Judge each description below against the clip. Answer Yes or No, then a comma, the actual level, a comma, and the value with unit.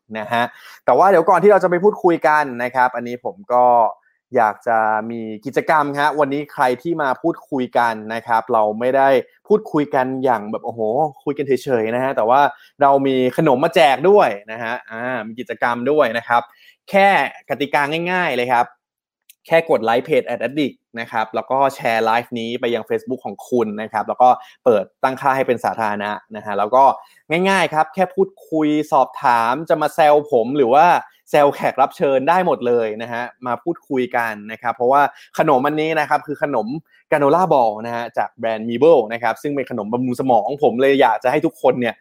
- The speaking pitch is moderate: No, low, 125 Hz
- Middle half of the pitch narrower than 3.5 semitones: No, average, 4.4 semitones